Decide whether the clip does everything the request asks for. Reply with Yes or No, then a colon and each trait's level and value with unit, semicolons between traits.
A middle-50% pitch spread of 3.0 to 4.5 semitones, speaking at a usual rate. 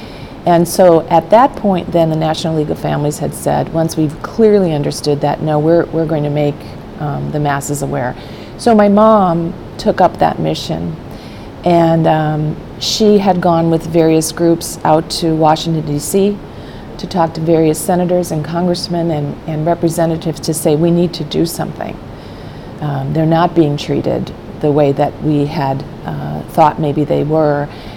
No: narrow, 2.5 semitones; average, 170 wpm